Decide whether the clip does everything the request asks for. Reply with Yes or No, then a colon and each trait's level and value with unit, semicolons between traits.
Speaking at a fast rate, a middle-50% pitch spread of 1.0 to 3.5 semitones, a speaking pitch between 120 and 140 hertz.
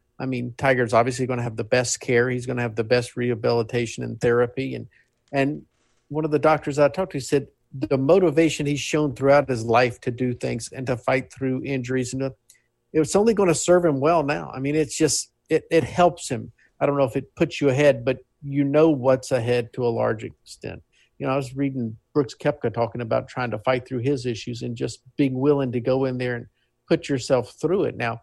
Yes: fast, 225 wpm; average, 2.9 semitones; low, 130 Hz